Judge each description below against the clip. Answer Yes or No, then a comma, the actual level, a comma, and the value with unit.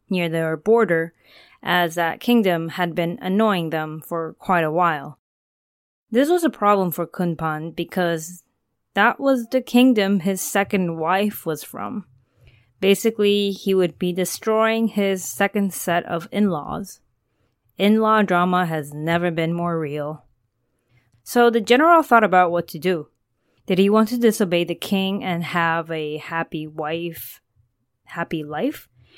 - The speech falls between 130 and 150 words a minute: Yes, average, 140 wpm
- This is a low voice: No, medium, 175 Hz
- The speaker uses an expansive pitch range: No, average, 4.3 semitones